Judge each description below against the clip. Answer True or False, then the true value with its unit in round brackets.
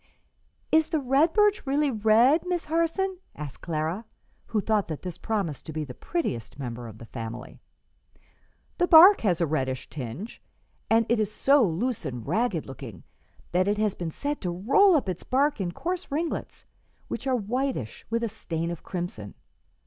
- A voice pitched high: True (210 Hz)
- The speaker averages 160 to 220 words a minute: True (175 wpm)